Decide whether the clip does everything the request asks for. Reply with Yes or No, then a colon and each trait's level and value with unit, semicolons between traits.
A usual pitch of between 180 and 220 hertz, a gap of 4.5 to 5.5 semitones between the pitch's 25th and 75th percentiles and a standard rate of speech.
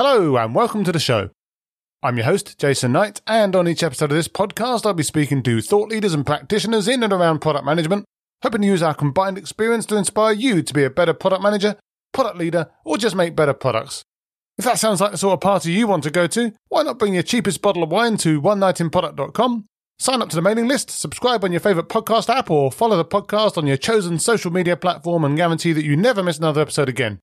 No: high, 190 Hz; average, 5.2 semitones; fast, 235 wpm